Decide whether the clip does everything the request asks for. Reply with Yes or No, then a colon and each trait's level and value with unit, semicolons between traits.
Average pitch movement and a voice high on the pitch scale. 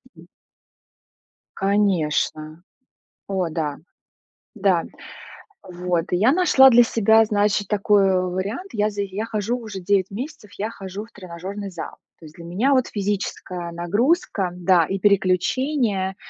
Yes: average, 3.2 semitones; high, 200 Hz